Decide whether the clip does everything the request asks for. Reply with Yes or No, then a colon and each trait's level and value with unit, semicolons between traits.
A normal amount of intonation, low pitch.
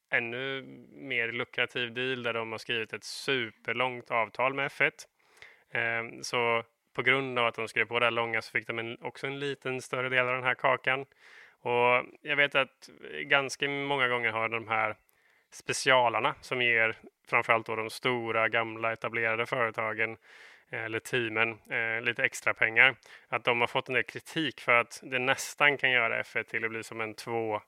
No: narrow, 2.2 semitones; low, 120 Hz